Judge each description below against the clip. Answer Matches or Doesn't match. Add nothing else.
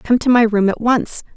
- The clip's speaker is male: Doesn't match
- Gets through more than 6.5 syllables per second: Doesn't match